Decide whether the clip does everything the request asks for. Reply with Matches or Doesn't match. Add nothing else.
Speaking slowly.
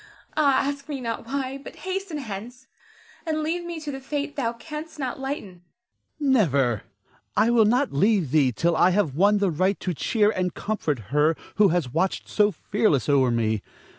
Doesn't match